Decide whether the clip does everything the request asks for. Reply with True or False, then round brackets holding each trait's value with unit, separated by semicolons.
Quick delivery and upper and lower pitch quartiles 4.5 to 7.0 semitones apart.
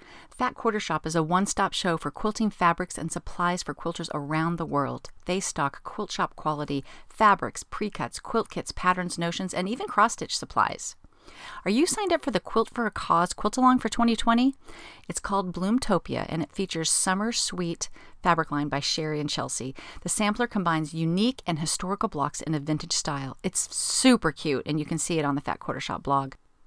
False (195 wpm; 5.2 semitones)